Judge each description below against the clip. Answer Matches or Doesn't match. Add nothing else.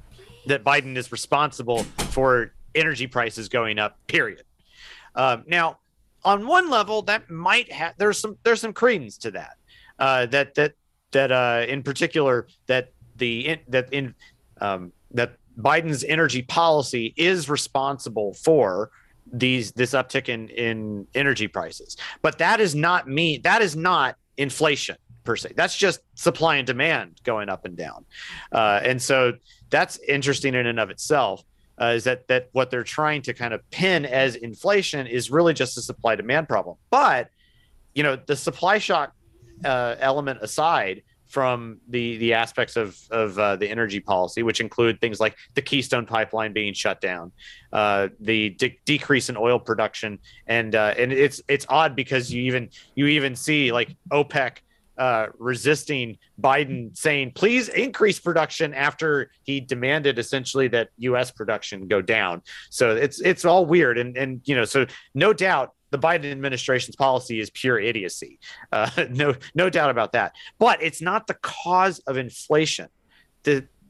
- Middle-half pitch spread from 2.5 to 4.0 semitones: Doesn't match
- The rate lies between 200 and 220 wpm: Doesn't match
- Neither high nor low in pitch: Doesn't match